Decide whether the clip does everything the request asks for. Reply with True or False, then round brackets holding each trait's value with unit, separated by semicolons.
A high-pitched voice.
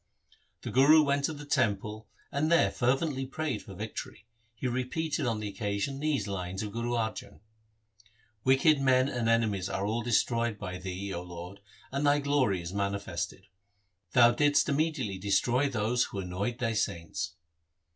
False (115 Hz)